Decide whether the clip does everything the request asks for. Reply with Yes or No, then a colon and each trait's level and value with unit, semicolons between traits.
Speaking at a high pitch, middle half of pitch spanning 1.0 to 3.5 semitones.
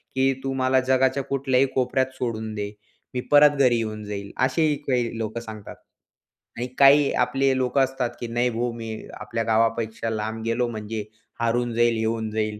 No: low, 120 Hz; average, 2.9 semitones